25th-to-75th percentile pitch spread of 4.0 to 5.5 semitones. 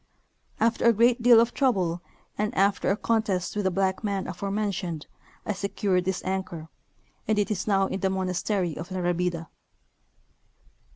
No: narrow, 2.6 semitones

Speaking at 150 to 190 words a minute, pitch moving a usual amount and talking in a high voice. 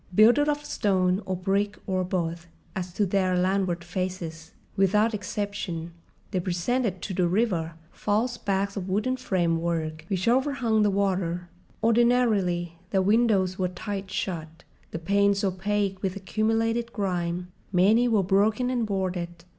No: slow, 135 wpm; average, 3.1 semitones; high, 195 Hz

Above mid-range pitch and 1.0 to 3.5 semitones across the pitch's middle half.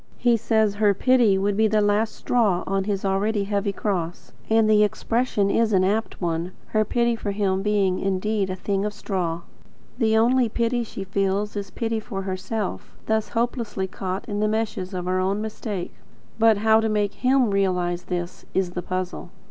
Yes: high, 205 Hz; narrow, 2.5 semitones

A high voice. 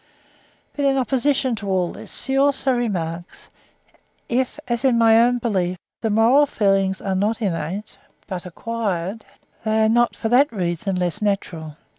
Yes: high, 220 Hz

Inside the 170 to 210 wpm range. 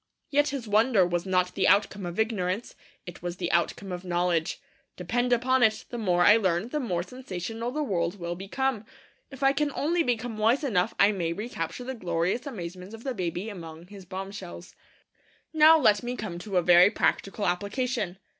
Yes: average, 185 wpm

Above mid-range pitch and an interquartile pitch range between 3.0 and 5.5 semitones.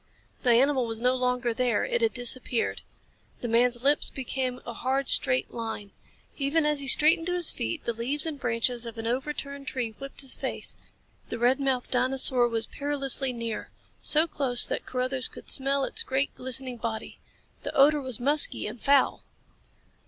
No: very high, 255 Hz; narrow, 2.6 semitones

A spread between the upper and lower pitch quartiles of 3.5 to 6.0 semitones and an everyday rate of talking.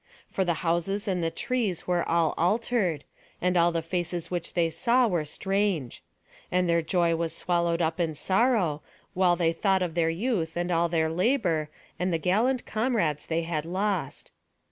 No: average, 2.8 semitones; average, 175 wpm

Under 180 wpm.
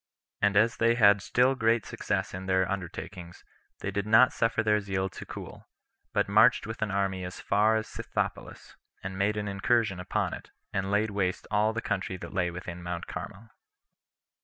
No: average, 185 wpm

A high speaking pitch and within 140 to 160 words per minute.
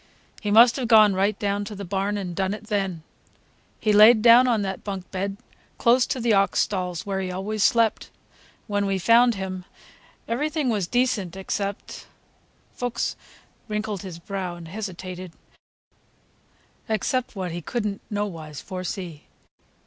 Yes: high, 200 Hz; average, 145 wpm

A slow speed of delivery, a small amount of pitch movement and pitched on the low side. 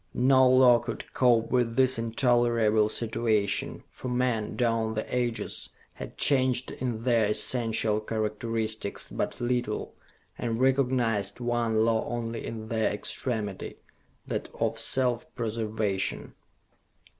Yes: slow, 115 wpm; narrow, 2.0 semitones; low, 115 Hz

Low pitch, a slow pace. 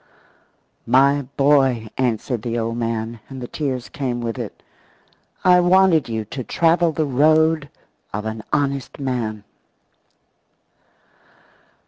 Yes: low, 130 Hz; slow, 115 wpm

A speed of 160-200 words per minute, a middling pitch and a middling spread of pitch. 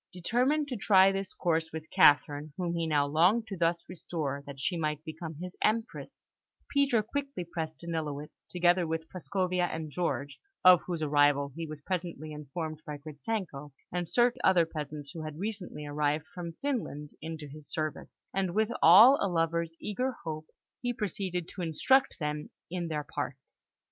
Yes: average, 165 wpm; medium, 165 Hz; average, 3.8 semitones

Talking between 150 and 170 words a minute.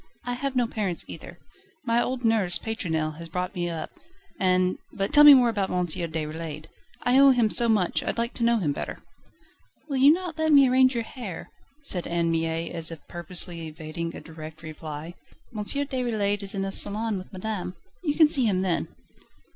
No: average, 195 wpm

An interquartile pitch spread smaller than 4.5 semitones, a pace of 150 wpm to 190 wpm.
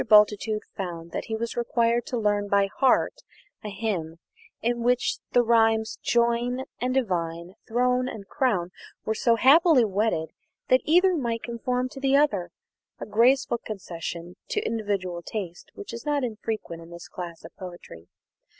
No: average, 4.9 semitones; average, 155 wpm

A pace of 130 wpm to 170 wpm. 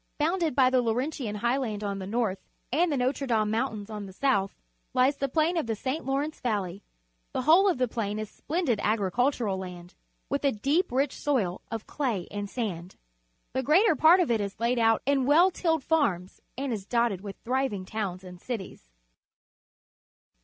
No: average, 185 wpm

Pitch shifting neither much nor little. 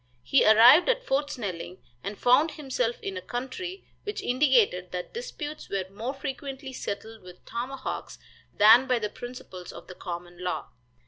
No: wide, 5.7 semitones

